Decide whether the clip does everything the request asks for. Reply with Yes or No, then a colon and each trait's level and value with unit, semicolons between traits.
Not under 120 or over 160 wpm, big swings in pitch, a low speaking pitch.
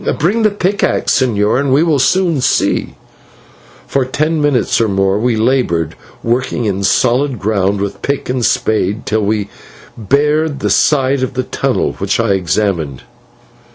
Yes: average, 155 wpm; wide, 5.7 semitones; low, 125 Hz